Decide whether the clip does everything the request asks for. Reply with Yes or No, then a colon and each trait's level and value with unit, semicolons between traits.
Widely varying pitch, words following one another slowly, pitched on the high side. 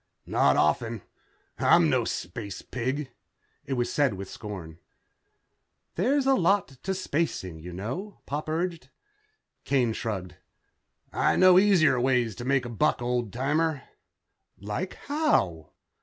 No: wide, 7.9 semitones; slow, 125 wpm; low, 130 Hz